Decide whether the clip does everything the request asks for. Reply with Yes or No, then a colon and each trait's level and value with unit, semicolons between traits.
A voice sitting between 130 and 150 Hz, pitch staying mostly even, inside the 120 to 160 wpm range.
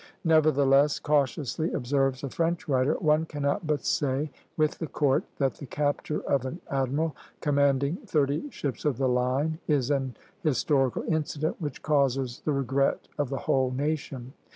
Yes: medium, 140 Hz; narrow, 2.3 semitones; average, 155 wpm